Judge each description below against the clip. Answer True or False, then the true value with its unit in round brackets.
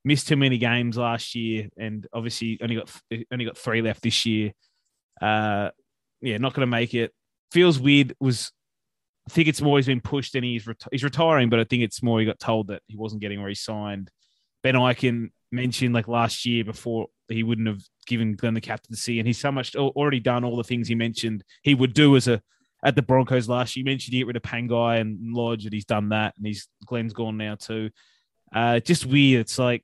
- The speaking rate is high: True (225 wpm)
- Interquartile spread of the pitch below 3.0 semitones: True (2.5 semitones)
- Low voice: True (120 Hz)